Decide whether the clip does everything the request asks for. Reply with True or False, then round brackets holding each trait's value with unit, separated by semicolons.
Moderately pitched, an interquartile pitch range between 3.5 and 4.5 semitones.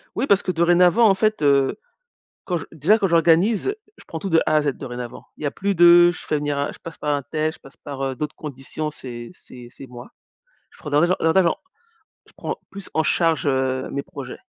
True (155 Hz; 4.1 semitones)